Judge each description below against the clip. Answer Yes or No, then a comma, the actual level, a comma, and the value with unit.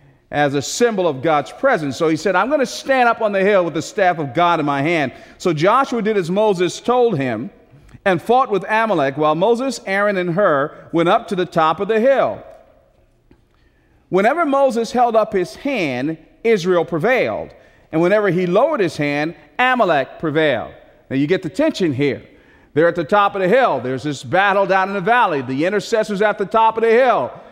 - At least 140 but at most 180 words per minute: No, average, 200 wpm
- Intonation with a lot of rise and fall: Yes, wide, 6.0 semitones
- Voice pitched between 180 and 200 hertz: Yes, high, 190 Hz